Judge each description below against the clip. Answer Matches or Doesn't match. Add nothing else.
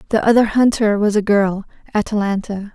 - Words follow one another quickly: Doesn't match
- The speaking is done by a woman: Matches